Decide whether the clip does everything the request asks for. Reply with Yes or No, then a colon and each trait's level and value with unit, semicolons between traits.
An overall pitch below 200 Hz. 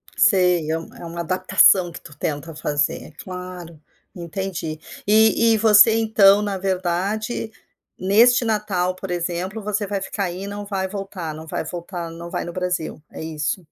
Yes: medium, 185 Hz